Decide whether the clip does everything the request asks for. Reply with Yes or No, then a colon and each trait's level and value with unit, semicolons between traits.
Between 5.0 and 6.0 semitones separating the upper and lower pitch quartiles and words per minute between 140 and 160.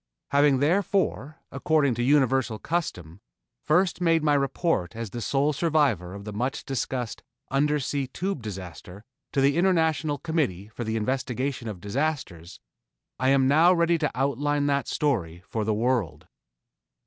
Yes: wide, 5.5 semitones; average, 145 wpm